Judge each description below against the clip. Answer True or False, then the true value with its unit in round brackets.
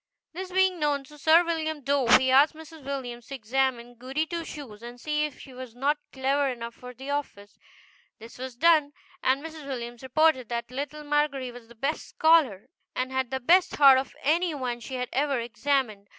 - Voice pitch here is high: True (270 Hz)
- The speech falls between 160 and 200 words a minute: True (195 wpm)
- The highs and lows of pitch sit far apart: False (3.5 semitones)